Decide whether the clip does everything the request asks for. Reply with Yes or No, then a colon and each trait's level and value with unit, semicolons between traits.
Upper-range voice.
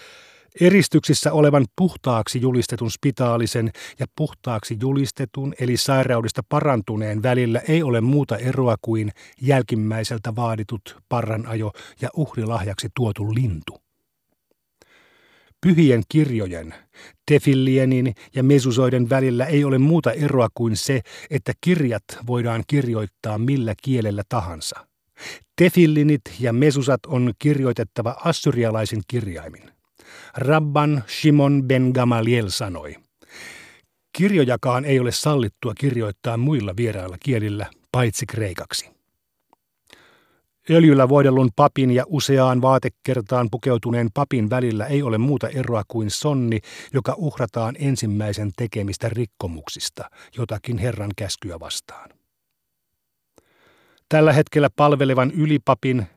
No: low, 125 Hz